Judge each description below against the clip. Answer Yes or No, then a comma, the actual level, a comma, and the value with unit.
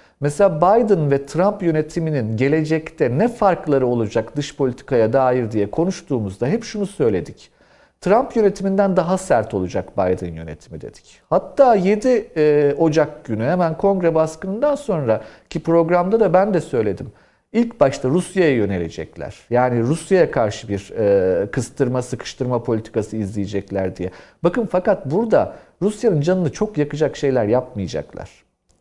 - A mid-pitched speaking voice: Yes, medium, 155 Hz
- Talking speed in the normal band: Yes, average, 125 wpm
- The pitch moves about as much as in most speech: No, wide, 8.1 semitones